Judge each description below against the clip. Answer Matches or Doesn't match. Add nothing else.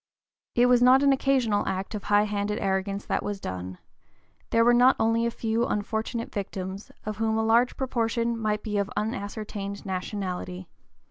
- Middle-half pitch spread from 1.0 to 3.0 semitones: Matches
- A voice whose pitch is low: Doesn't match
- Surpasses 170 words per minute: Doesn't match